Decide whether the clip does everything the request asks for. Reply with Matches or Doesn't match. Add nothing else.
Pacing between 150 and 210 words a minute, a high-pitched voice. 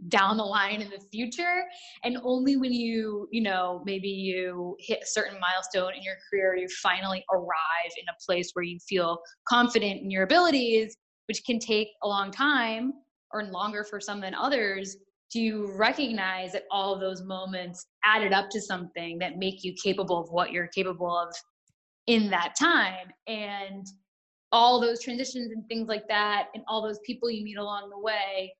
Matches